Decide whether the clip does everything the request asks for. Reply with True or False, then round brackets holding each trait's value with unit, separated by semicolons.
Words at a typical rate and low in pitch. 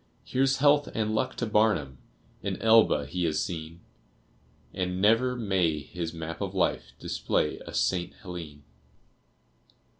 False (130 wpm; 90 Hz)